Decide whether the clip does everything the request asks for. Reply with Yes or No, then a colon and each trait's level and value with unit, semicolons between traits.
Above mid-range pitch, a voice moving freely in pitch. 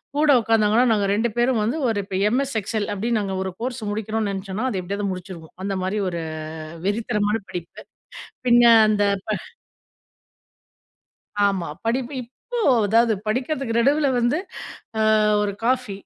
No: high, 220 Hz; average, 3.3 semitones